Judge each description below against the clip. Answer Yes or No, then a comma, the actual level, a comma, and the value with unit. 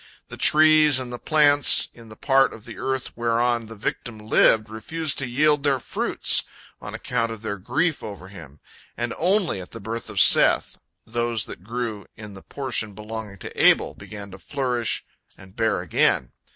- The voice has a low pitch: Yes, low, 115 Hz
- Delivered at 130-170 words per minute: No, average, 180 wpm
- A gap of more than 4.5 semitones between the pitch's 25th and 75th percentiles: No, average, 4.0 semitones